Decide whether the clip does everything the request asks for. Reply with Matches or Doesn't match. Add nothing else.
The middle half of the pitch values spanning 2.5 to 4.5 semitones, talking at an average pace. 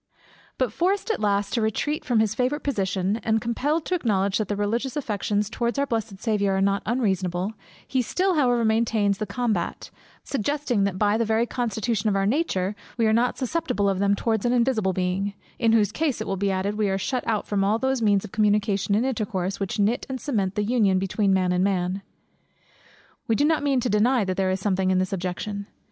Doesn't match